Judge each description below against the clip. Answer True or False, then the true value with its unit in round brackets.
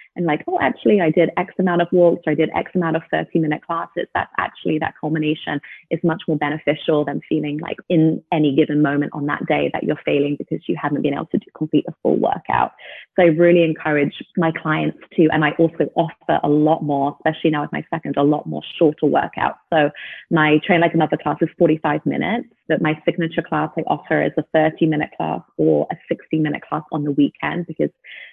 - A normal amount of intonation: False (1.9 semitones)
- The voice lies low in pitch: False (155 Hz)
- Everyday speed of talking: False (220 wpm)